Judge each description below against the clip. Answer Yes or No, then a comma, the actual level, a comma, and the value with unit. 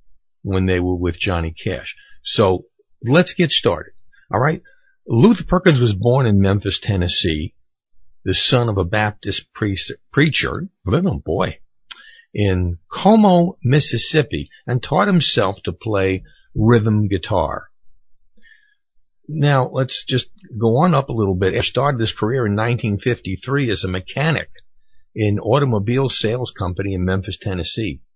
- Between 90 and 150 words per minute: Yes, slow, 135 wpm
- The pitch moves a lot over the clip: Yes, wide, 7.0 semitones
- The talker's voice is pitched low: Yes, low, 115 Hz